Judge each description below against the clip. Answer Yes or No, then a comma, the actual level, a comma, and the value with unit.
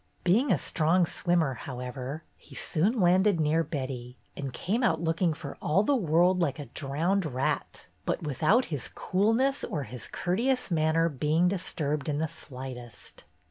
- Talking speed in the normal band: Yes, average, 155 wpm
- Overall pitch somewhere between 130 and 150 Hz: No, medium, 160 Hz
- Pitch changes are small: No, average, 4.6 semitones